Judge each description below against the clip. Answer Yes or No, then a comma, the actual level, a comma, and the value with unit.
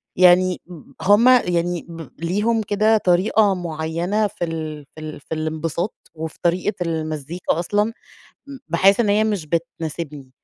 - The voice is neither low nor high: Yes, medium, 175 Hz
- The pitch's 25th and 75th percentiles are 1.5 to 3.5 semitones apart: No, average, 4.2 semitones